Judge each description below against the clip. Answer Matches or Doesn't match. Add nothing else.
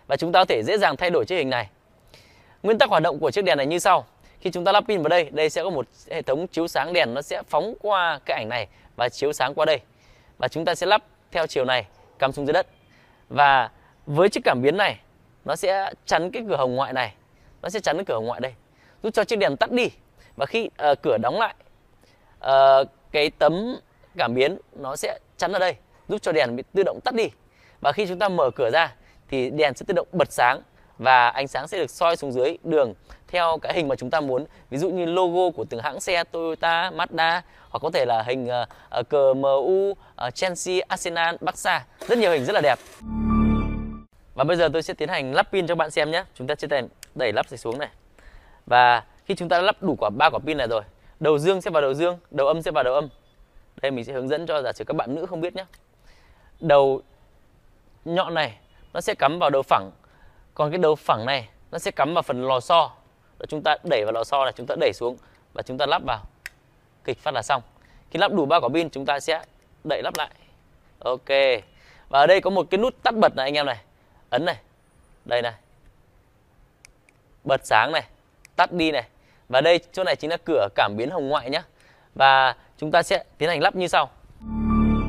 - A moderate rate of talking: Matches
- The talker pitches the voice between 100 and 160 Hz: Matches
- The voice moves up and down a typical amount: Doesn't match